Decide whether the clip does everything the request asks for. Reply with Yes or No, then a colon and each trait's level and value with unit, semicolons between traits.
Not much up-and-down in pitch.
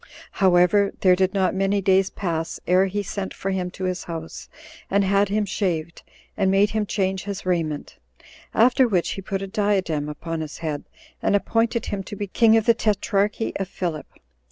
Yes: narrow, 2.3 semitones